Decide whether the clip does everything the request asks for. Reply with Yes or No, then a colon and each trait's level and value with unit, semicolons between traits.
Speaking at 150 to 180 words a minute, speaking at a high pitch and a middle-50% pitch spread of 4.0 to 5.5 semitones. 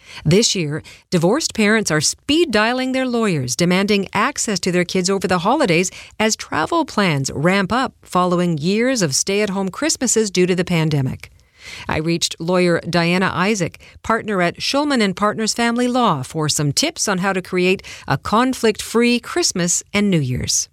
Yes: average, 160 wpm; high, 195 Hz; average, 4.5 semitones